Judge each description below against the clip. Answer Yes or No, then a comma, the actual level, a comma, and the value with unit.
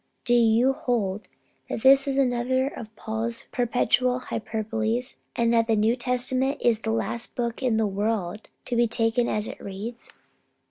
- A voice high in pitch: Yes, high, 235 Hz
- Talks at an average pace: Yes, average, 170 wpm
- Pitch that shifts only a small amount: Yes, narrow, 2.0 semitones